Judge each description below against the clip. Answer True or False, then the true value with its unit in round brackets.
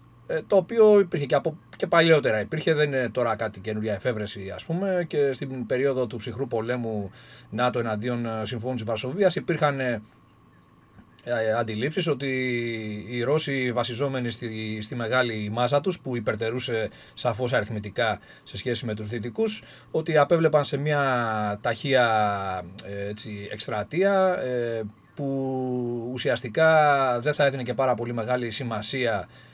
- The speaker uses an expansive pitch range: False (4.3 semitones)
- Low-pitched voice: True (125 Hz)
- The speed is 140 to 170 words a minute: False (125 wpm)